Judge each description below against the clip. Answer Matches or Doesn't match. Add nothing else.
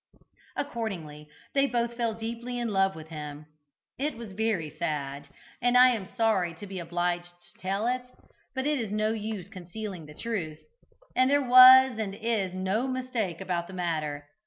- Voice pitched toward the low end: Doesn't match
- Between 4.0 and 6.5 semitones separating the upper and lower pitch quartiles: Matches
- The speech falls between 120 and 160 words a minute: Doesn't match